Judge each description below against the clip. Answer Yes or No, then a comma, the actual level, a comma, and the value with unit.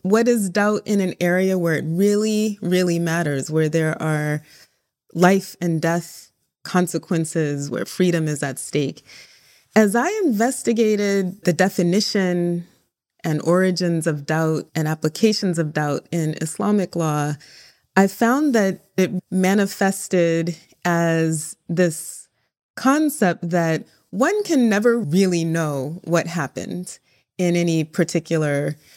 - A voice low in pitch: No, medium, 175 Hz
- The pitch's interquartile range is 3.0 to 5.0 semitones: Yes, average, 3.4 semitones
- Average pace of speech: No, slow, 120 wpm